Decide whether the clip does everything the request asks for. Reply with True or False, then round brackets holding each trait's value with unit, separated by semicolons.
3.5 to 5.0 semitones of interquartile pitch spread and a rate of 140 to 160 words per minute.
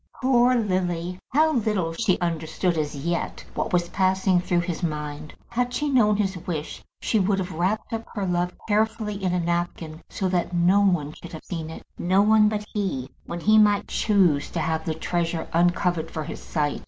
False (4.1 semitones; 190 wpm)